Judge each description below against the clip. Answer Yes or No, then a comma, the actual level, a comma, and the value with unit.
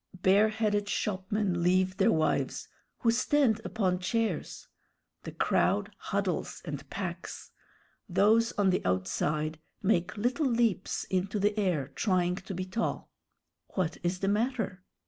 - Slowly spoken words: Yes, slow, 125 wpm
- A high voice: Yes, high, 195 Hz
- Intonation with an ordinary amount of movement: Yes, average, 3.3 semitones